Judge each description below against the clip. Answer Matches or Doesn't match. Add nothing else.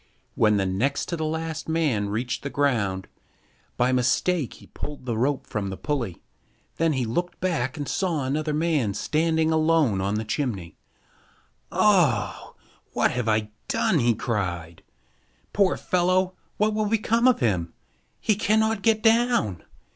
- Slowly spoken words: Doesn't match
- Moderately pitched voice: Matches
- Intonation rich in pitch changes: Matches